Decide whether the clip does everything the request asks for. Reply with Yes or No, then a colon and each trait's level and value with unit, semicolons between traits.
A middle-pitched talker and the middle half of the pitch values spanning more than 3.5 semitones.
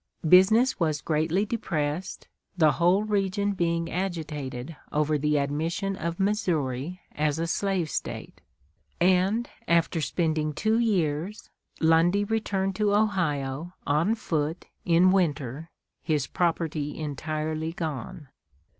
Yes: medium, 165 Hz; average, 4.0 semitones